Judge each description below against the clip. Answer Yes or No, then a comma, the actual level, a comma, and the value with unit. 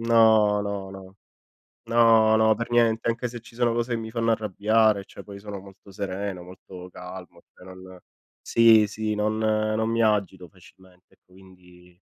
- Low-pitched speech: Yes, low, 105 Hz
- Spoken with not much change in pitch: No, average, 3.1 semitones